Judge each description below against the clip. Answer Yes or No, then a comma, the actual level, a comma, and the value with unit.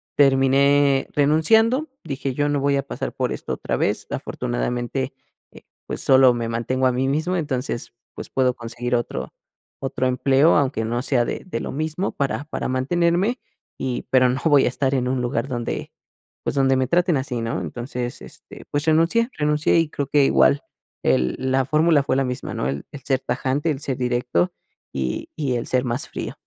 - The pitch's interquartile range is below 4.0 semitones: Yes, average, 2.9 semitones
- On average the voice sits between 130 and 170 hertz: Yes, low, 135 Hz